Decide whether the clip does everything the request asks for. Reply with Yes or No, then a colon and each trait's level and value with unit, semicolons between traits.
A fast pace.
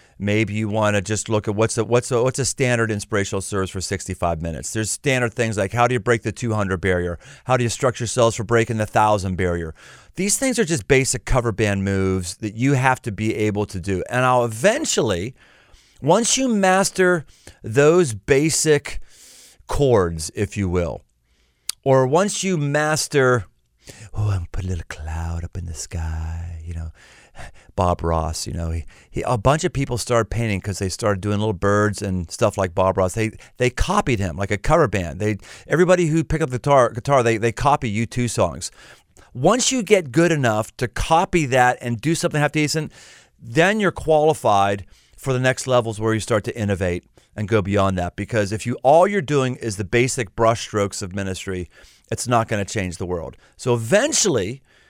No: average, 195 wpm